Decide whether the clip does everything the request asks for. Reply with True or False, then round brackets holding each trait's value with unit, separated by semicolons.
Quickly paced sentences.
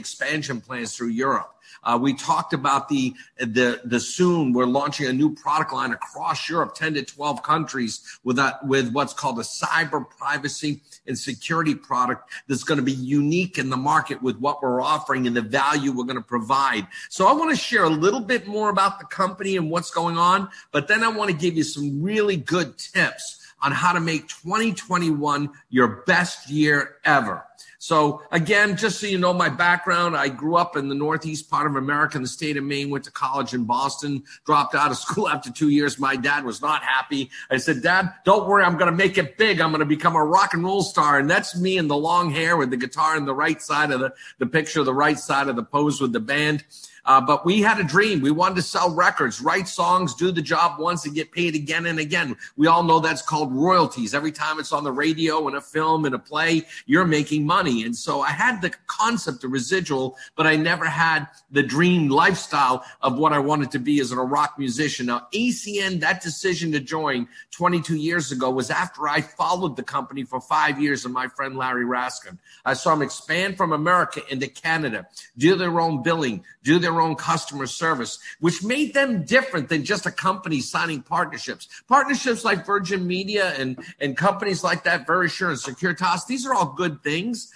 True (215 wpm)